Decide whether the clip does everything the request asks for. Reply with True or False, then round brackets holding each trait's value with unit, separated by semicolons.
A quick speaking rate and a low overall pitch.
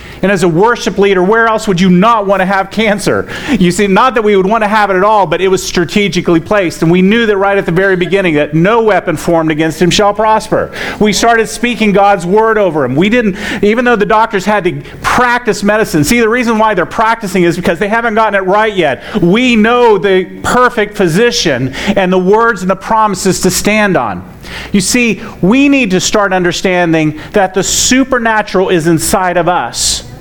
False (215 wpm; 200 Hz)